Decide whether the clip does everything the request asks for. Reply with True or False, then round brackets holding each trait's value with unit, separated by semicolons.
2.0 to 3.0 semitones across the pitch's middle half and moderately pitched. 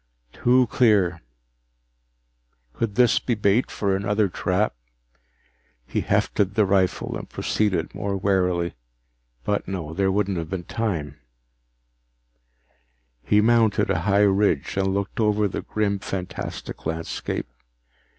False (2.4 semitones; 100 Hz)